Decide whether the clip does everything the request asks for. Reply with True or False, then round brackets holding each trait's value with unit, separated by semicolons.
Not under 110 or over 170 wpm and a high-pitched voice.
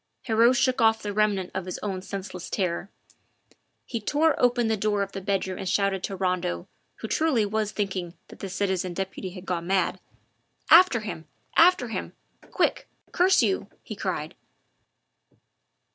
True (160 wpm; 200 Hz)